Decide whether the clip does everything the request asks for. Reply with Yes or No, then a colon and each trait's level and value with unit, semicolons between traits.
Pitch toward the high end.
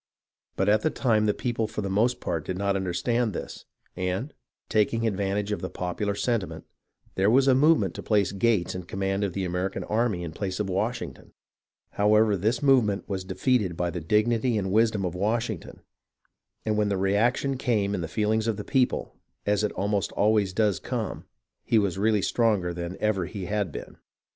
No: low, 105 Hz